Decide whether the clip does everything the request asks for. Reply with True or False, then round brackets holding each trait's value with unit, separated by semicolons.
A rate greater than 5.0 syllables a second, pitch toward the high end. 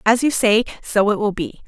True (5.3 syllables/s; 220 Hz)